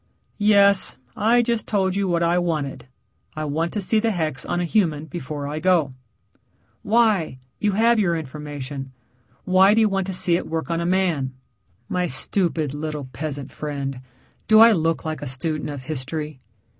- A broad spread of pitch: No, average, 4.8 semitones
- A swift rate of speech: No, average, 175 wpm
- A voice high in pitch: No, medium, 165 Hz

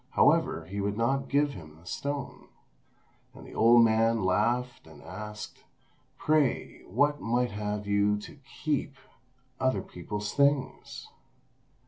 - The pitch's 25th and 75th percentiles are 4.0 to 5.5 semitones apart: Yes, average, 5.0 semitones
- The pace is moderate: No, slow, 125 wpm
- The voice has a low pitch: Yes, low, 115 Hz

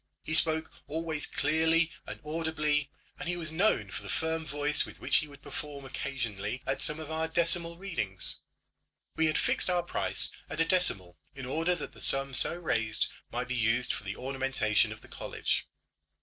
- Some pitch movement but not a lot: Yes, average, 3.9 semitones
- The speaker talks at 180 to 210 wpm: Yes, average, 185 wpm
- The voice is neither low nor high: Yes, medium, 150 Hz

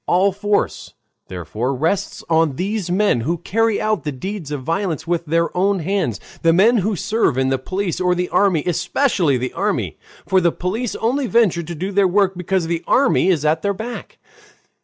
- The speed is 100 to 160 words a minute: No, average, 190 wpm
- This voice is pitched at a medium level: Yes, medium, 180 Hz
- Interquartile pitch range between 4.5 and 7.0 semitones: No, average, 3.9 semitones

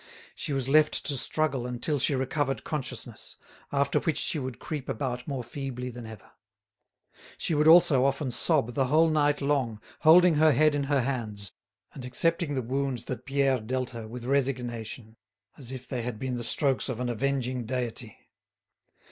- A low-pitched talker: Yes, low, 130 Hz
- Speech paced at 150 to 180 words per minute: Yes, average, 175 wpm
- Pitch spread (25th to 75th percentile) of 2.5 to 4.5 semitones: Yes, average, 2.8 semitones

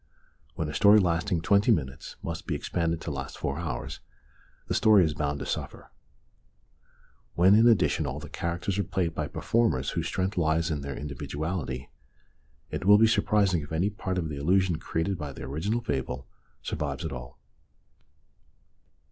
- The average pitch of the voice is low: Yes, very low, 85 Hz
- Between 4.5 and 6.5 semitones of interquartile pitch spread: Yes, average, 5.0 semitones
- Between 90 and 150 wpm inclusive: No, average, 165 wpm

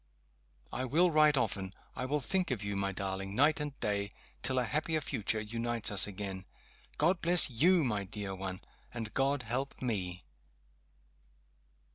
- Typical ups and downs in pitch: No, wide, 6.8 semitones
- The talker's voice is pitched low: Yes, low, 120 Hz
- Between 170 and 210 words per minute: No, average, 155 wpm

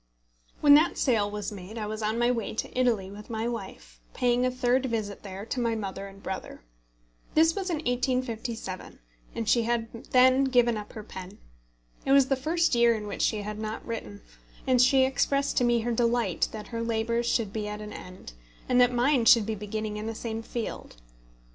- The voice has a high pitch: Yes, high, 230 Hz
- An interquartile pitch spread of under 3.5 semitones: Yes, average, 2.9 semitones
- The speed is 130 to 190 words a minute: No, fast, 205 wpm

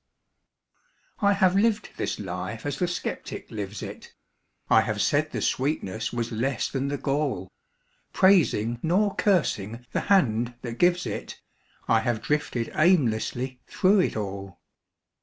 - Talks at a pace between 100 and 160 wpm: Yes, average, 140 wpm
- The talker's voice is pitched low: Yes, low, 130 Hz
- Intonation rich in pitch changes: Yes, wide, 8.0 semitones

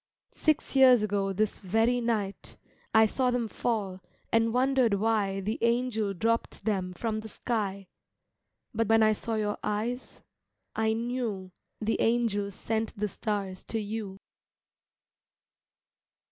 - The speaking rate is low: Yes, slow, 130 wpm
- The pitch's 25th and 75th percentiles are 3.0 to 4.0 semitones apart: No, narrow, 2.4 semitones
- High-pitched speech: Yes, high, 220 Hz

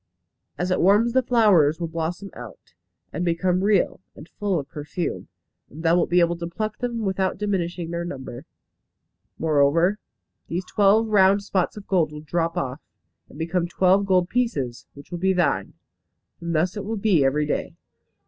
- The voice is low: No, medium, 175 Hz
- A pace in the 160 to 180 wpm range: Yes, average, 175 wpm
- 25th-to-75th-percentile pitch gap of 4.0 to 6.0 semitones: No, average, 3.4 semitones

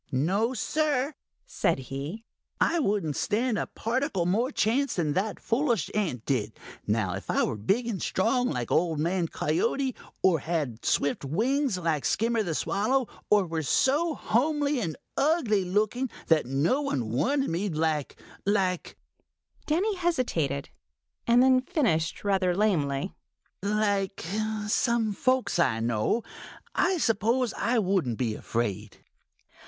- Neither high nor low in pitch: No, high, 200 Hz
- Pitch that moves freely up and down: Yes, wide, 8.2 semitones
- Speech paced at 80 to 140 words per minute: Yes, slow, 135 wpm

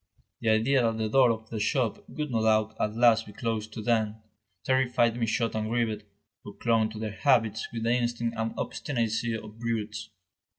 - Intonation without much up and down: Yes, narrow, 1.4 semitones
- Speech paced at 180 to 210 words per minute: Yes, average, 185 wpm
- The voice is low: Yes, low, 115 Hz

